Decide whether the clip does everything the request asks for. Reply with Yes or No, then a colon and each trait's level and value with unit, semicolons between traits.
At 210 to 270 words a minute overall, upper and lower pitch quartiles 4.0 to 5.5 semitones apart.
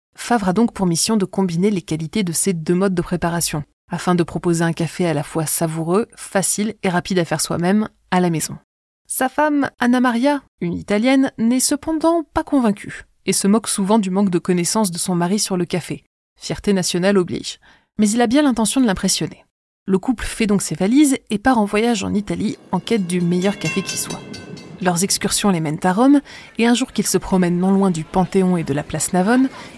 Yes: average, 215 wpm; average, 4.7 semitones